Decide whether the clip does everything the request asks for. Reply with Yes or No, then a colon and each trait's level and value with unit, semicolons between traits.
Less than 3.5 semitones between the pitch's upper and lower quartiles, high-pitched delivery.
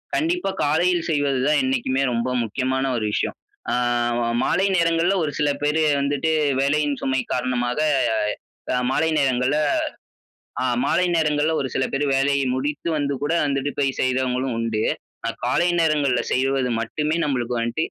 No: average, 2.9 semitones; medium, 140 Hz